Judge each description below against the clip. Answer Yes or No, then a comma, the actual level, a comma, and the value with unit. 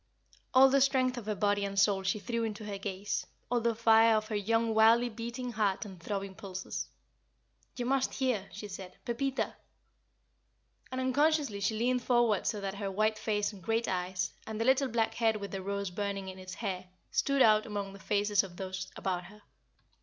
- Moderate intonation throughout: Yes, average, 3.0 semitones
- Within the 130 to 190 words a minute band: No, average, 200 wpm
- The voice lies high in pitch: Yes, high, 215 Hz